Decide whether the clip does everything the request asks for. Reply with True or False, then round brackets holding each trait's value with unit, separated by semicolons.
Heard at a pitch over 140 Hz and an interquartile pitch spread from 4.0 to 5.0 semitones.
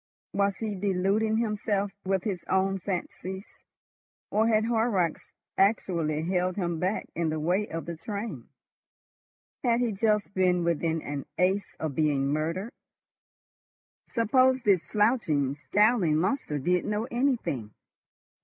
True (190 Hz; 4.4 semitones)